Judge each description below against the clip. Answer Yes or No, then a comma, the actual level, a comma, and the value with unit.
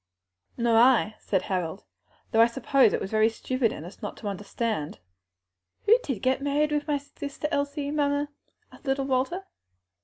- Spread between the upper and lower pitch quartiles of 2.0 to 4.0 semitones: No, average, 4.6 semitones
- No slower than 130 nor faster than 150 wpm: No, average, 165 wpm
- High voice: Yes, very high, 260 Hz